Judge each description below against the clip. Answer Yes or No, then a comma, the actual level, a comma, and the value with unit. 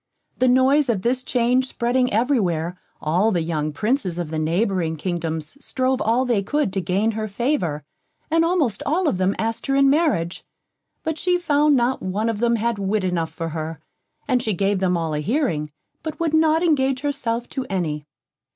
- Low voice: No, high, 225 Hz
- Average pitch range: No, wide, 7.2 semitones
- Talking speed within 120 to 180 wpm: No, average, 190 wpm